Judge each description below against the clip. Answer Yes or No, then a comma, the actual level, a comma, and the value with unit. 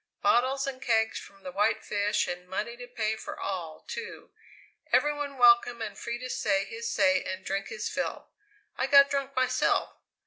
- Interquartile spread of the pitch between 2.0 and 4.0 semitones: No, average, 4.5 semitones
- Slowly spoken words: No, average, 180 wpm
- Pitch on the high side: Yes, high, 230 Hz